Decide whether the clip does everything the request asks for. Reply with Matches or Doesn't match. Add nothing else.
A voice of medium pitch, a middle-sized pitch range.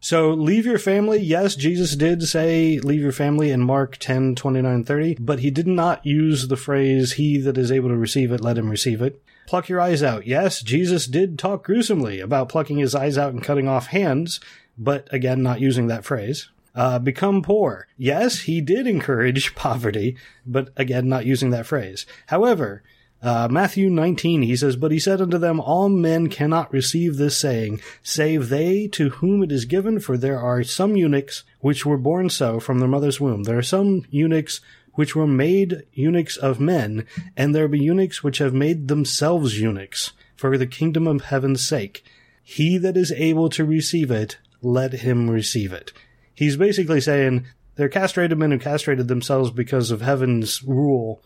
Matches